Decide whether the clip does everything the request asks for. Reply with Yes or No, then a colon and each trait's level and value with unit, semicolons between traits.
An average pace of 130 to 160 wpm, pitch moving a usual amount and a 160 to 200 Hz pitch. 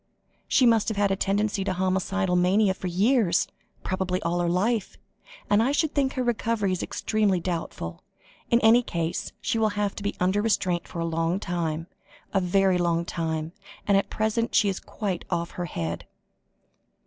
No: average, 180 wpm; average, 3.6 semitones; high, 190 Hz